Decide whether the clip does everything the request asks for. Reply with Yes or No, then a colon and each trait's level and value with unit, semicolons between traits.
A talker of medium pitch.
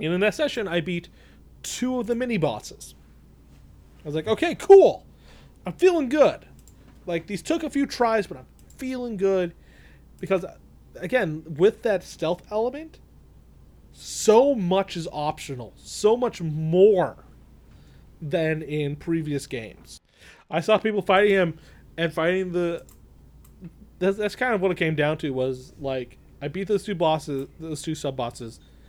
Yes: medium, 170 Hz